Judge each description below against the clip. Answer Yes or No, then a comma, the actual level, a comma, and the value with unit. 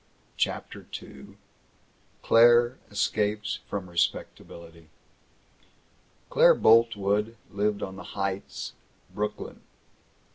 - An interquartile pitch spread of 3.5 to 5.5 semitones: No, narrow, 2.4 semitones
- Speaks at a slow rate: Yes, slow, 75 wpm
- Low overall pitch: Yes, low, 105 Hz